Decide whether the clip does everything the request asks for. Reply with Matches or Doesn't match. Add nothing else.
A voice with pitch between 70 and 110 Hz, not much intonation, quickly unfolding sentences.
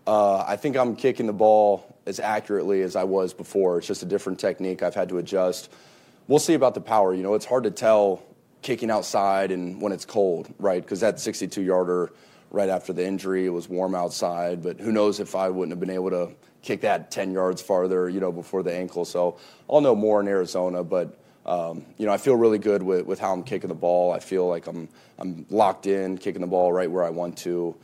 Matches